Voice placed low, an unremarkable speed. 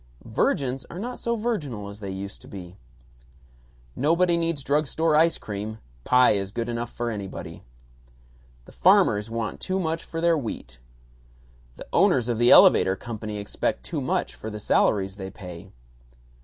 Yes: low, 115 Hz; average, 160 wpm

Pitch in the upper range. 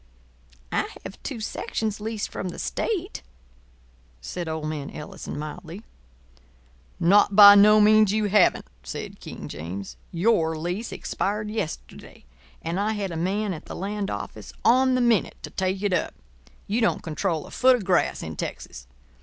Yes: high, 195 Hz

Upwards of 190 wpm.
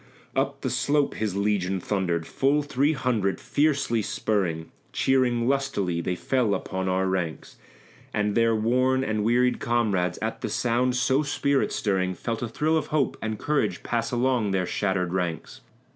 No: average, 160 wpm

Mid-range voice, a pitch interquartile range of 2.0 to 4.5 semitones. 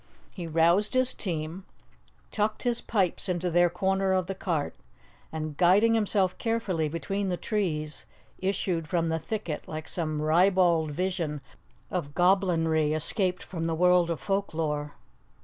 Yes: medium, 175 Hz; average, 3.3 semitones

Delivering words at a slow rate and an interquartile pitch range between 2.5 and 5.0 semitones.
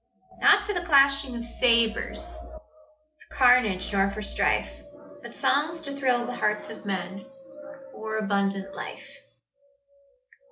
No: slow, 130 wpm; wide, 5.6 semitones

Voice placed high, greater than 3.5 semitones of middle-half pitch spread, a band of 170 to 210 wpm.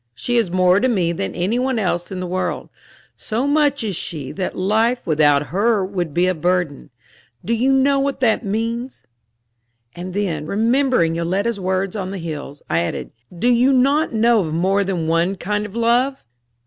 Yes: high, 195 Hz; average, 5.2 semitones; average, 185 wpm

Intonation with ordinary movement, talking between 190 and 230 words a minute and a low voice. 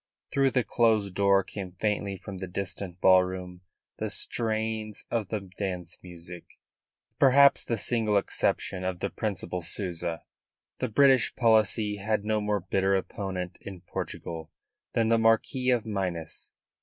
No: average, 3.4 semitones; average, 145 wpm; low, 100 Hz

